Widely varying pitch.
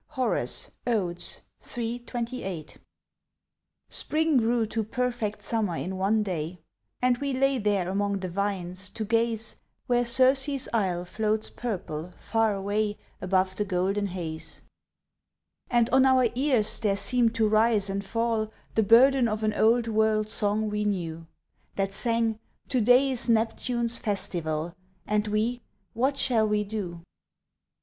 No: average, 3.3 semitones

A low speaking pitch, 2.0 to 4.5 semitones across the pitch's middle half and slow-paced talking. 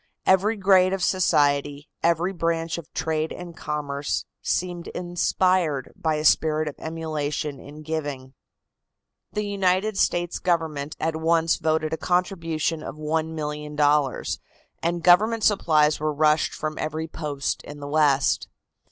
No: medium, 160 Hz; average, 2.7 semitones; slow, 130 wpm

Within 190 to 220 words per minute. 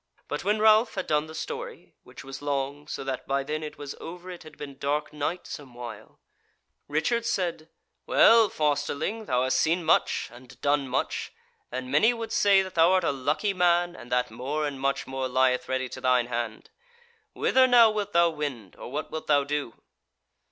Yes: average, 195 wpm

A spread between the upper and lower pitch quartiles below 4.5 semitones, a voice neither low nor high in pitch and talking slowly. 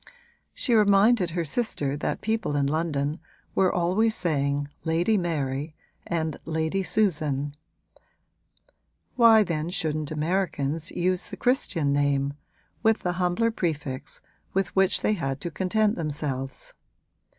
No: average, 5.0 semitones; medium, 165 Hz; slow, 120 wpm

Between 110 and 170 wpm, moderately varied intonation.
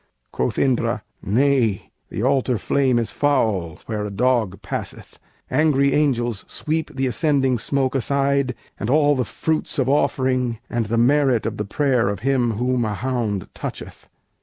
Yes: average, 155 wpm; average, 3.7 semitones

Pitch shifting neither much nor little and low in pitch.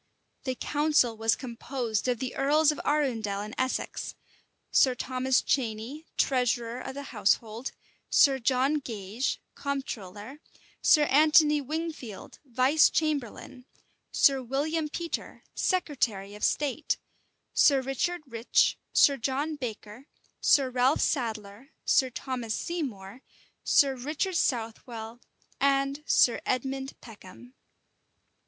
No: average, 3.8 semitones; very high, 260 Hz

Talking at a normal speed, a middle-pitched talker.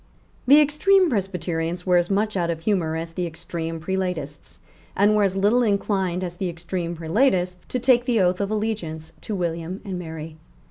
Yes: average, 180 wpm; medium, 180 Hz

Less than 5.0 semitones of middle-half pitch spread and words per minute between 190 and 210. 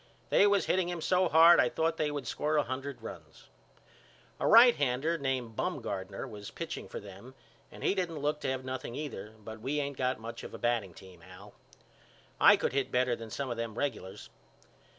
No: average, 5.3 semitones; average, 195 wpm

